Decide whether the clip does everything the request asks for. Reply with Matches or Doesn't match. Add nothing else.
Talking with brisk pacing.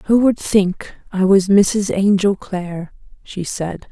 Doesn't match